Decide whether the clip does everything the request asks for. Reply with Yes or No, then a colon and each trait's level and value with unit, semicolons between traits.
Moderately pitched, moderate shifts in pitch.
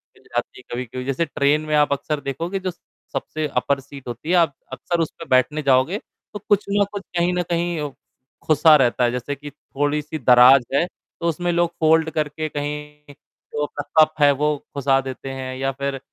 Yes: medium, 150 Hz; average, 3.1 semitones